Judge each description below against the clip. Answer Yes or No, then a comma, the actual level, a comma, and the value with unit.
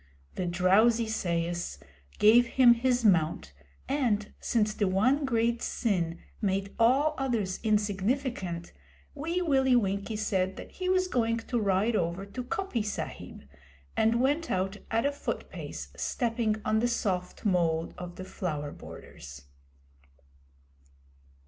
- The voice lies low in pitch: No, high, 215 Hz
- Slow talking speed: Yes, slow, 130 wpm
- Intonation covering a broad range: No, average, 4.7 semitones